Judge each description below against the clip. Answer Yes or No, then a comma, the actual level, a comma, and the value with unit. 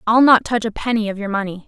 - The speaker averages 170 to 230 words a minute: No, fast, 285 wpm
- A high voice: Yes, high, 215 Hz